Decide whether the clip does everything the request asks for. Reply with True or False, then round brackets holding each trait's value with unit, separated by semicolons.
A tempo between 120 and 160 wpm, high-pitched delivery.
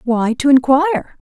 True (135 wpm; 275 Hz)